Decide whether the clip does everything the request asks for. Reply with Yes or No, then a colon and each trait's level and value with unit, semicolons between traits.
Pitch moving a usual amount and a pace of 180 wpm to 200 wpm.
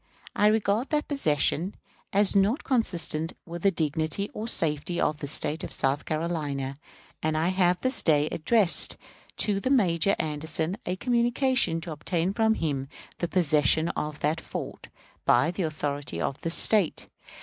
No: average, 4.8 semitones; average, 150 wpm